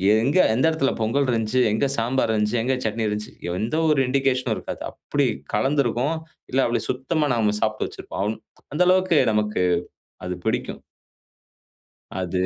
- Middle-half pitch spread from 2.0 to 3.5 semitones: No, average, 4.2 semitones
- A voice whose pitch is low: Yes, low, 120 Hz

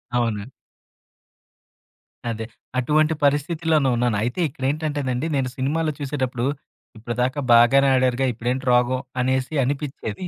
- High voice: No, low, 130 Hz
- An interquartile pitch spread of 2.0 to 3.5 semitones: Yes, average, 2.9 semitones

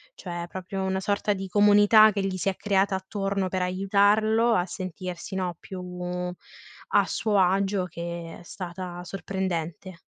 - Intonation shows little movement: Yes, narrow, 1.9 semitones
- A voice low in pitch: No, high, 190 Hz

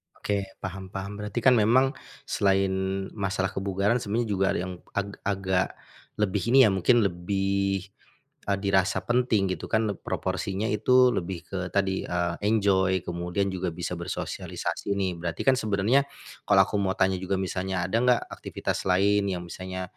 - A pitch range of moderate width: No, narrow, 1.7 semitones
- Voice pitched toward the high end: No, very low, 95 Hz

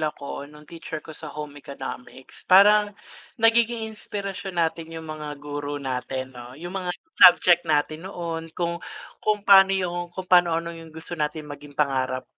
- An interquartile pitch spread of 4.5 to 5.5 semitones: No, average, 4.0 semitones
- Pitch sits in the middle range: Yes, medium, 165 Hz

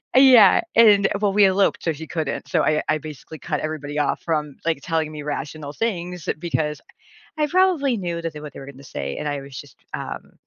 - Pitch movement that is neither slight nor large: Yes, average, 4.7 semitones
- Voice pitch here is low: No, medium, 160 Hz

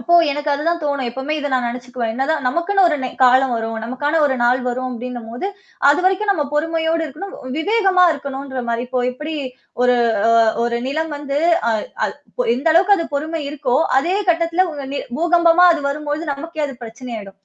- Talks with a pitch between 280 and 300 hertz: Yes, very high, 290 Hz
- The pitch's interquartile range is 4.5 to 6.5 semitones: Yes, average, 4.8 semitones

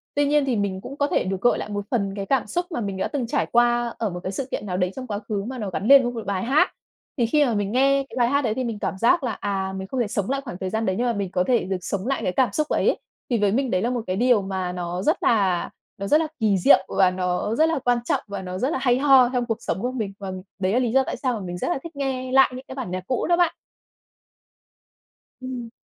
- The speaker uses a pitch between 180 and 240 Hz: Yes, high, 230 Hz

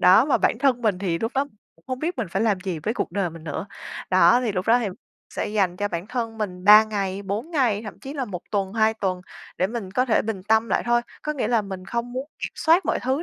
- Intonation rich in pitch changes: No, average, 4.3 semitones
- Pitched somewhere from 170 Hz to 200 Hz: No, high, 215 Hz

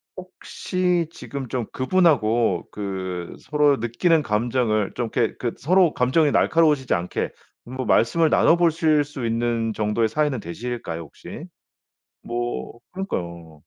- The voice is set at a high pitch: No, low, 120 Hz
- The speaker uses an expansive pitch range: Yes, wide, 6.1 semitones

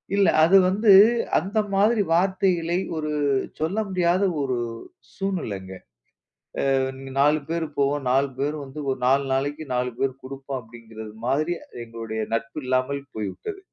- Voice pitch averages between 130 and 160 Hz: Yes, medium, 140 Hz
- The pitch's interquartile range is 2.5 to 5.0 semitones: No, wide, 5.5 semitones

